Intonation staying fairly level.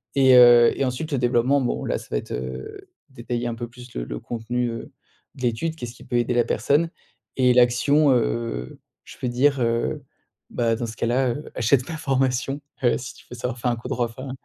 Yes: narrow, 1.9 semitones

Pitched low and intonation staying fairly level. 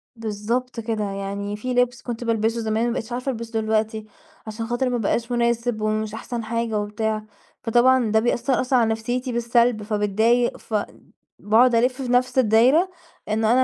No: high, 230 Hz; narrow, 2.0 semitones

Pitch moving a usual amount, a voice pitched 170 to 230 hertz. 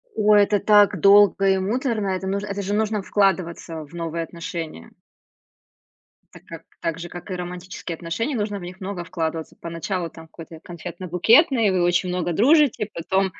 Yes: average, 3.3 semitones; medium, 185 Hz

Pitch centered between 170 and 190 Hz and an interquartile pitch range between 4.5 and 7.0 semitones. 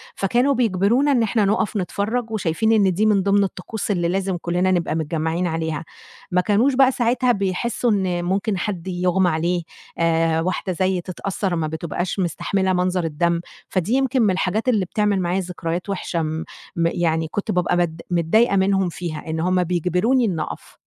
No: medium, 185 Hz; average, 3.4 semitones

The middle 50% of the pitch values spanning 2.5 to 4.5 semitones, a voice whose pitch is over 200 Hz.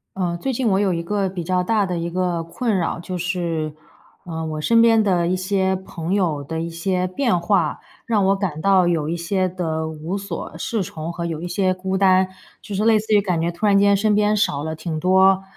No: average, 2.9 semitones; medium, 185 Hz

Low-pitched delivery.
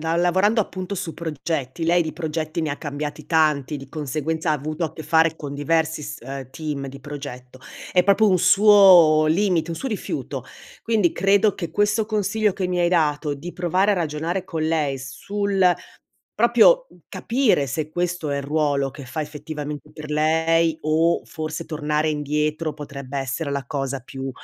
No: medium, 155 Hz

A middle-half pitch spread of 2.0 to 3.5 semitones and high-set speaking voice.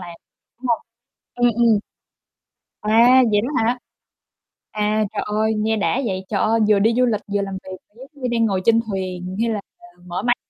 Yes: average, 2.8 semitones; high, 215 Hz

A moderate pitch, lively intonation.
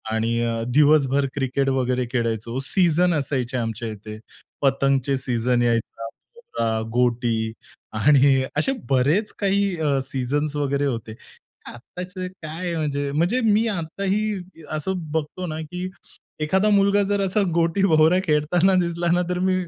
Yes: medium, 150 Hz; wide, 6.4 semitones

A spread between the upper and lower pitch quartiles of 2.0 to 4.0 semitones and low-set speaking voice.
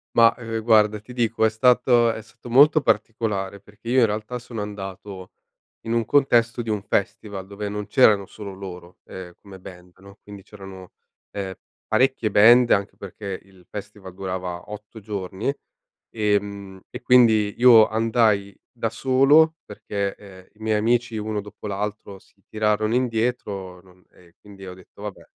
Yes: average, 2.8 semitones; low, 105 Hz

